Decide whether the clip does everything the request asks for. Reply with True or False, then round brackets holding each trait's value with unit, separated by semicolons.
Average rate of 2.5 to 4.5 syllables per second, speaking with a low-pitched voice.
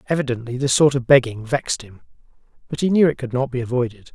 False (6.7 syllables/s; 130 Hz)